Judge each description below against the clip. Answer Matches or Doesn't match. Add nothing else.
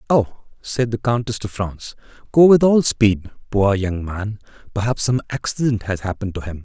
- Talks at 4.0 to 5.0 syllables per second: Matches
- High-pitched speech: Doesn't match